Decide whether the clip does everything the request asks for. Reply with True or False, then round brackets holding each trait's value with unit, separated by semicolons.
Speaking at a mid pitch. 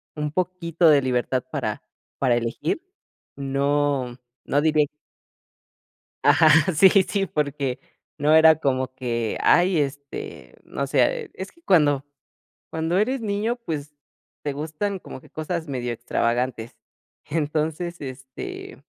True (150 Hz)